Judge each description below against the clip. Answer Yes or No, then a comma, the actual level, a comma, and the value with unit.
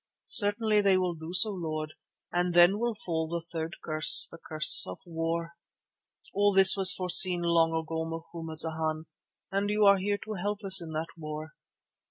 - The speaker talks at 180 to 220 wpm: No, average, 170 wpm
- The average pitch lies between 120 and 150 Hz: No, medium, 170 Hz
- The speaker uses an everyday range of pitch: Yes, average, 3.3 semitones